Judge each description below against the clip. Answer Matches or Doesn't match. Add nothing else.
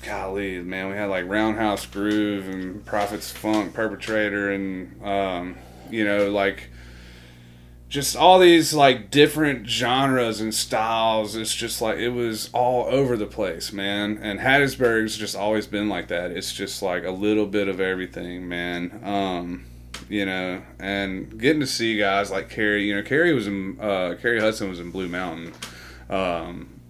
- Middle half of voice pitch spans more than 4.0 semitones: Doesn't match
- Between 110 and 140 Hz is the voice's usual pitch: Doesn't match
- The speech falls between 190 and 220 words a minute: Doesn't match